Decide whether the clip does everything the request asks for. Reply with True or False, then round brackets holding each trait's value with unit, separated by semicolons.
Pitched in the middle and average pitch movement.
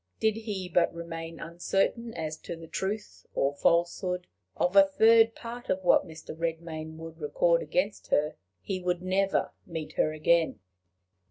True (170 Hz; 3.1 semitones)